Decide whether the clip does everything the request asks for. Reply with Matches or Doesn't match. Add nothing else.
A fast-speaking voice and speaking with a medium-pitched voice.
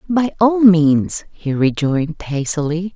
Doesn't match